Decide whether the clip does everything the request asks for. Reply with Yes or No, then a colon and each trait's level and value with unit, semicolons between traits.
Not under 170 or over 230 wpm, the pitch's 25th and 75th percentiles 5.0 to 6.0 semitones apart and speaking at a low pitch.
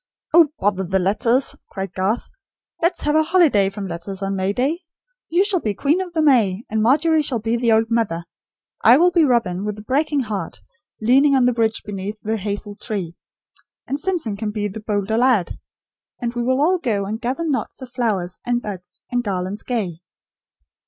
No: average, 195 wpm; wide, 5.4 semitones; high, 225 Hz